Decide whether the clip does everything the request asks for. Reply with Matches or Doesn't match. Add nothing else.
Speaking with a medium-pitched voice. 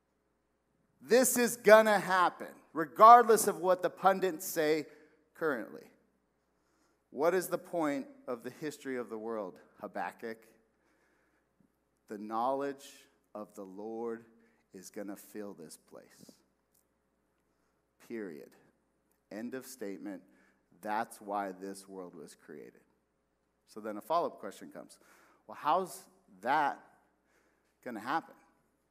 Doesn't match